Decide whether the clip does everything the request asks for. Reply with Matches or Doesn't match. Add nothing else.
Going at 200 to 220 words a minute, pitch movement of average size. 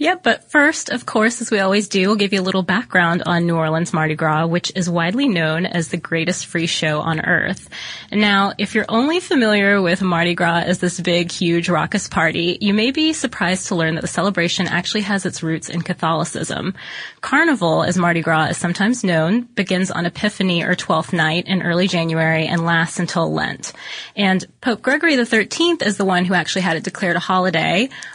Matches